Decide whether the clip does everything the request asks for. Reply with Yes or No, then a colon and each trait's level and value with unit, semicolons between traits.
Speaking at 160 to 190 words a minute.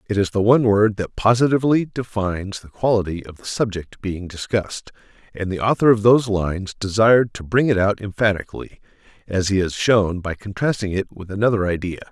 Yes: average, 185 wpm